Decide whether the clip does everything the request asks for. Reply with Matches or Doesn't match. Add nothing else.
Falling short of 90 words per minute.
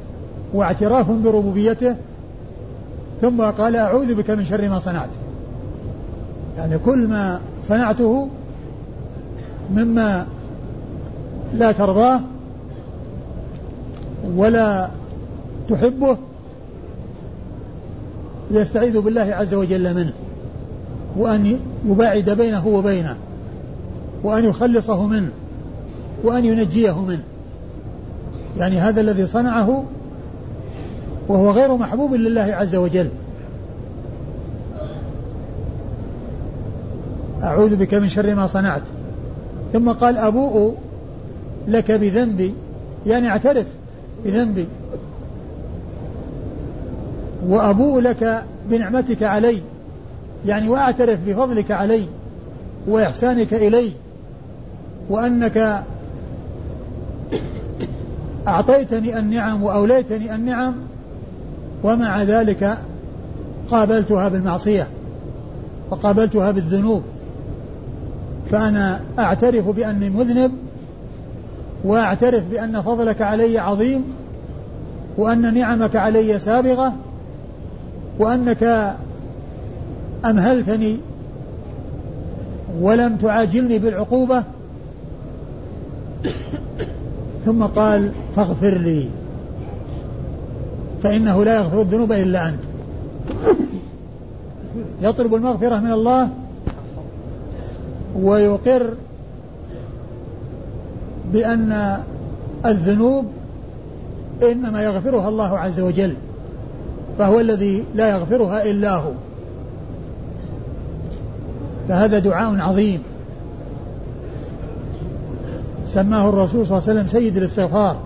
Matches